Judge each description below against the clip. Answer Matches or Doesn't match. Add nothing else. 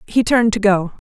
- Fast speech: Matches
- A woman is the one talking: Matches